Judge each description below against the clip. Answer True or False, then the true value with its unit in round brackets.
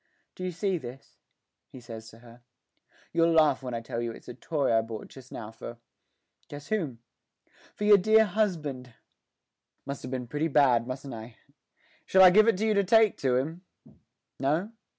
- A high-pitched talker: False (140 Hz)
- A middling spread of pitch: False (7.2 semitones)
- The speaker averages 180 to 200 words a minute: True (185 wpm)